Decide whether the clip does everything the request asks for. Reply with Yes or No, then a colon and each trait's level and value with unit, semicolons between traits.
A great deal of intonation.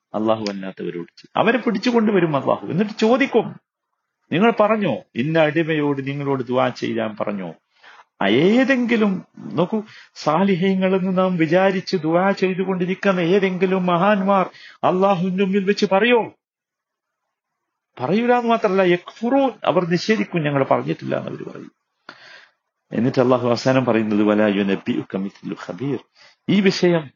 Yes: wide, 7.2 semitones